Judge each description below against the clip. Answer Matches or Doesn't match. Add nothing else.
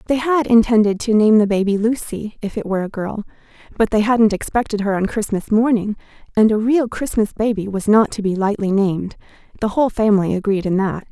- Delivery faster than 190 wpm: Matches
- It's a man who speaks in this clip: Doesn't match